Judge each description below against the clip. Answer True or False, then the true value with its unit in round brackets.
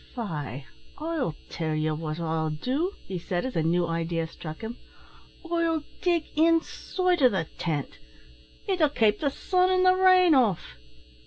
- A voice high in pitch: True (230 Hz)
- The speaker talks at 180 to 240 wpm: False (160 wpm)